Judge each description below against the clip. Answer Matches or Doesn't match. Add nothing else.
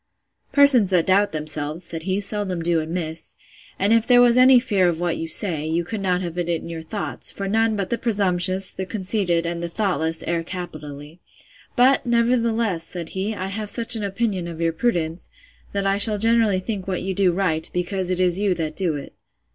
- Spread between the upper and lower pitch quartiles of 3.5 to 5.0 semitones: Matches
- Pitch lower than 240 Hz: Matches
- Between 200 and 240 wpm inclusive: Matches